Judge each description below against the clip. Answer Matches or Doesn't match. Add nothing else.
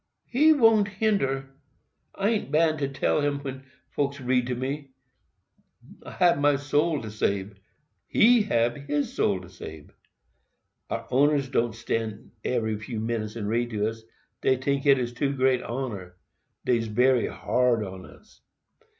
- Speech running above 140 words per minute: Doesn't match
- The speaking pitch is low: Matches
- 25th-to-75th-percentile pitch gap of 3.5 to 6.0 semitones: Matches